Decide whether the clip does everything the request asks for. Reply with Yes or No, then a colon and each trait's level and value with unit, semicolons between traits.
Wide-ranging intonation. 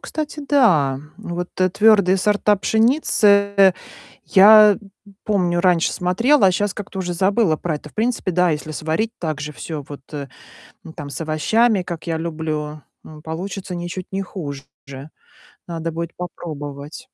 No: average, 4.5 semitones